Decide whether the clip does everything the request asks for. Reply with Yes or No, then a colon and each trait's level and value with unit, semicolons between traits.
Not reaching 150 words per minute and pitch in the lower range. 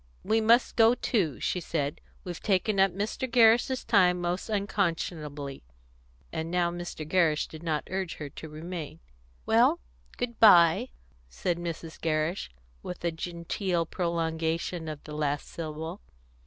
No: average, 140 wpm; medium, 170 Hz